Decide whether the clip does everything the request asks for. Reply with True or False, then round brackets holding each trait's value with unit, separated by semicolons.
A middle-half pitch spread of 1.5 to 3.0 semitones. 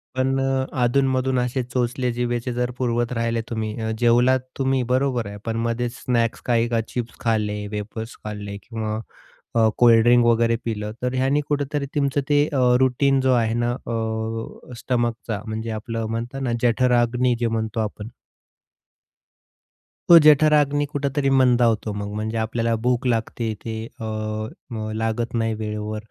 True (2.5 semitones)